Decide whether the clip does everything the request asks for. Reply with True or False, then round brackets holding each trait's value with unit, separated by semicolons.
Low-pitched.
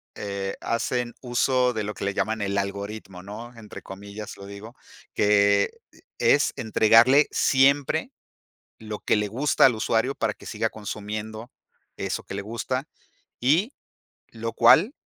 True (110 Hz)